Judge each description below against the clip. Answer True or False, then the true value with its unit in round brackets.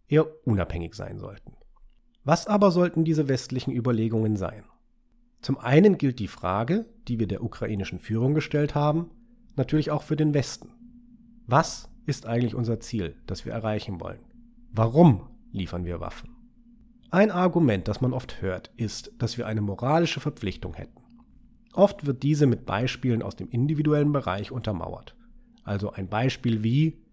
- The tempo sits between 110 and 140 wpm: False (150 wpm)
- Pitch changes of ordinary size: False (7.6 semitones)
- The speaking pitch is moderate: False (130 Hz)